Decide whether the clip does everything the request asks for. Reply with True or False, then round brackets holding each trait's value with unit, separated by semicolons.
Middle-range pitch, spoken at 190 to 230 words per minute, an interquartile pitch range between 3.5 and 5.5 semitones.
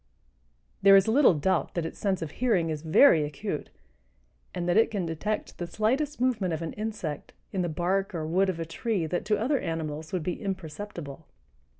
True (180 Hz; 195 wpm; 4.5 semitones)